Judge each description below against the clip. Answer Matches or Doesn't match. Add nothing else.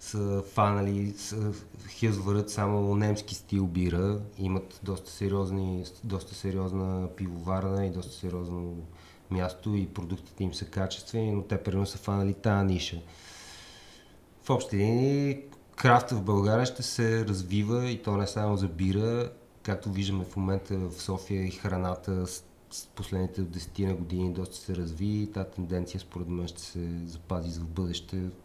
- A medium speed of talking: Matches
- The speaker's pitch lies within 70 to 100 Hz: Matches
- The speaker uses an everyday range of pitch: Doesn't match